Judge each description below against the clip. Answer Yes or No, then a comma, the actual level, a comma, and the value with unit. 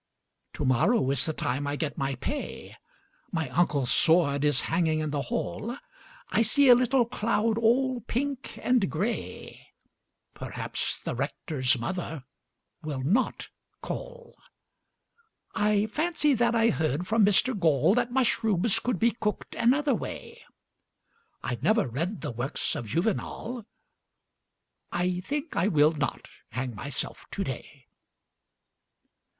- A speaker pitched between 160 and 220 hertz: Yes, high, 190 Hz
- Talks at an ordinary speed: No, slow, 125 wpm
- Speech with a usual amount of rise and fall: No, wide, 8.4 semitones